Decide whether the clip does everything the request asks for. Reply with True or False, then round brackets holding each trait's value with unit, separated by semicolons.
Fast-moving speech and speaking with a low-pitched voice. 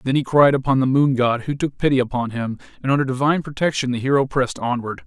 True (235 wpm; 130 Hz)